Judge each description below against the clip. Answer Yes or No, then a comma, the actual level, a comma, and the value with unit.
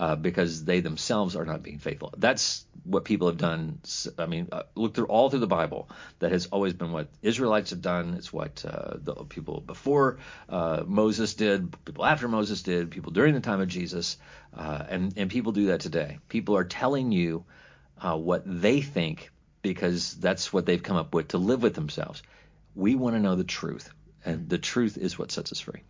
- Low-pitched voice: Yes, very low, 95 Hz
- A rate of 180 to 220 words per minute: Yes, fast, 205 wpm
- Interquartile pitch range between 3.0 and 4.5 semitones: Yes, average, 4.1 semitones